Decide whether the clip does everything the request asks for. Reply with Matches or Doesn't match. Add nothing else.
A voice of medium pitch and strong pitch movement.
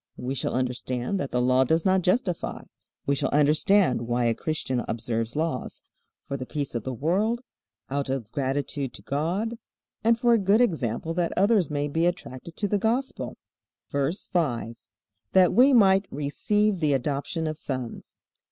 Matches